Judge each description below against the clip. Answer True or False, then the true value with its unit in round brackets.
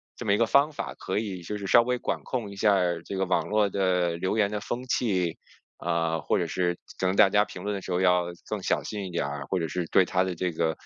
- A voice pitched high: False (95 Hz)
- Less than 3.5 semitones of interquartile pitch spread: True (2.8 semitones)